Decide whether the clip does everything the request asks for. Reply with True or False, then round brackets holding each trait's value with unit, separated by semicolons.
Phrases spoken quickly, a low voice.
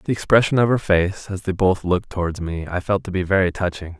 True (255 wpm; 95 Hz)